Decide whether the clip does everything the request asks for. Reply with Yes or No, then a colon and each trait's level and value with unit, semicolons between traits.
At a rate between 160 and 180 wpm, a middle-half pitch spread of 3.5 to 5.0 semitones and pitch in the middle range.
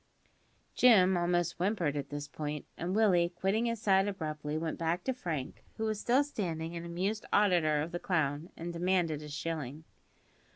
Yes: average, 170 wpm; average, 4.0 semitones; medium, 175 Hz